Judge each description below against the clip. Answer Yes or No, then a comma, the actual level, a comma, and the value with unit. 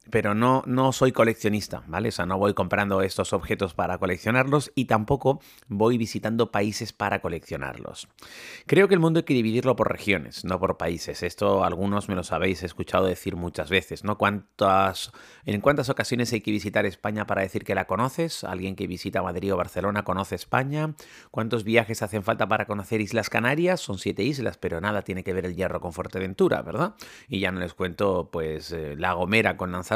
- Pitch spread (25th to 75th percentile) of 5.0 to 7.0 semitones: No, average, 3.5 semitones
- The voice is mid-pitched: No, low, 105 Hz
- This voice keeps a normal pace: No, fast, 195 wpm